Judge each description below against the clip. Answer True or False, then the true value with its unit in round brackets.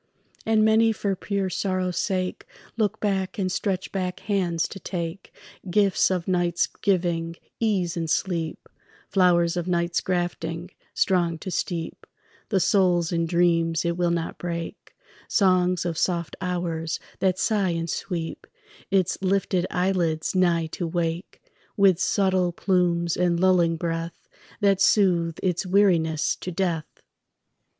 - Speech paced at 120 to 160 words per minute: True (135 wpm)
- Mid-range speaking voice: True (180 Hz)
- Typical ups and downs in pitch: False (2.1 semitones)